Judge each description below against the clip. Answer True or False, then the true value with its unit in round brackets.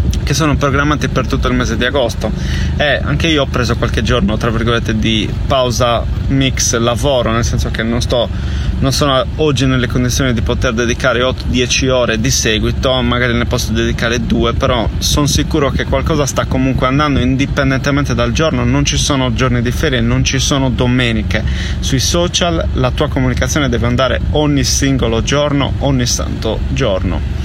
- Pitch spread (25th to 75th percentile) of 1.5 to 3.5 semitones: True (2.9 semitones)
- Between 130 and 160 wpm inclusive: False (170 wpm)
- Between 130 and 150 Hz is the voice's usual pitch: False (120 Hz)